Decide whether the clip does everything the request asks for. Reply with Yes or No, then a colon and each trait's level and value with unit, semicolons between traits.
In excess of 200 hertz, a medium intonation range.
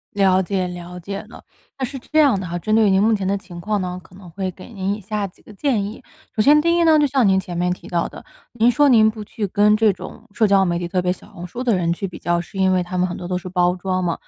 No: high, 195 Hz; average, 3.2 semitones